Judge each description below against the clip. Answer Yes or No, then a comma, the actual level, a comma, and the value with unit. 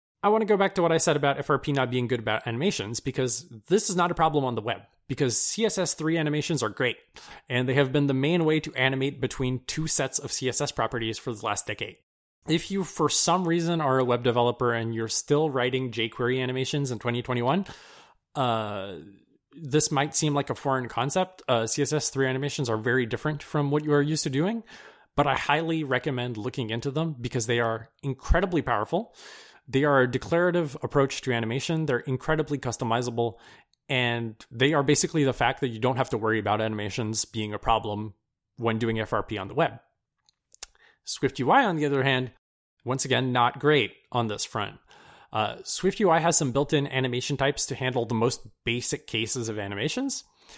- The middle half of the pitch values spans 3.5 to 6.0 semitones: Yes, average, 4.2 semitones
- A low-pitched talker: Yes, low, 130 Hz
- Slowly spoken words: No, average, 190 wpm